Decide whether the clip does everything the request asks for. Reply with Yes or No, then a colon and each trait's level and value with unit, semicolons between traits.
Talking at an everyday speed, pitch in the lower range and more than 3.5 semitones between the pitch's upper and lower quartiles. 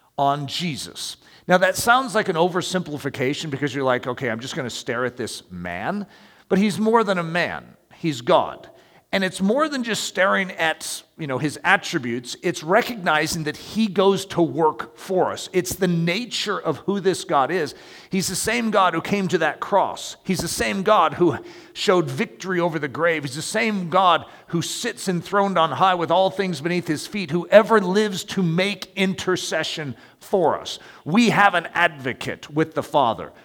No: average, 185 wpm; medium, 175 Hz; average, 4.0 semitones